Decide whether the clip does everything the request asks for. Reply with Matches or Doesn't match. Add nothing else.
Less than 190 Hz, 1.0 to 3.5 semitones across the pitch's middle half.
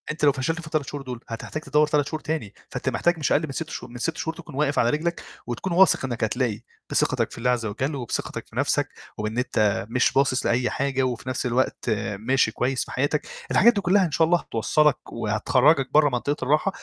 Doesn't match